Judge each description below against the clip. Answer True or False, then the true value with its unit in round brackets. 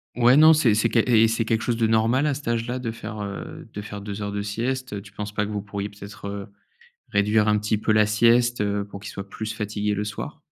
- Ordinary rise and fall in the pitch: False (2.2 semitones)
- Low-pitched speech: True (105 Hz)